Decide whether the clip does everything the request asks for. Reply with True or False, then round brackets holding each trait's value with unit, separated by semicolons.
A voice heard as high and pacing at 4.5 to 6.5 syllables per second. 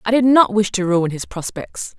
True (205 Hz; 4.8 syllables/s)